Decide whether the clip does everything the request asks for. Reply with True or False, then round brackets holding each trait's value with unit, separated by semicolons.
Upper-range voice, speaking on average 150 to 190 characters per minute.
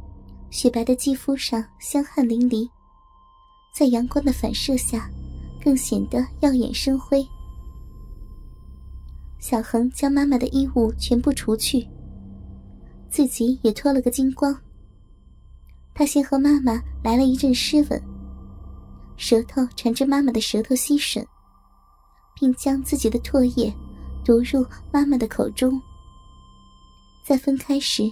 True (245 Hz; 180 characters per minute)